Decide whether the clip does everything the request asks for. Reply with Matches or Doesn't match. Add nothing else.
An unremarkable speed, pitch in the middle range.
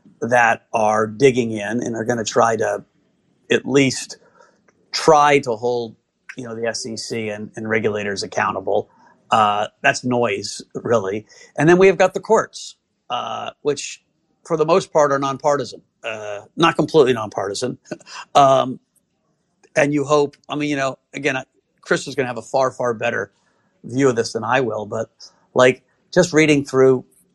Doesn't match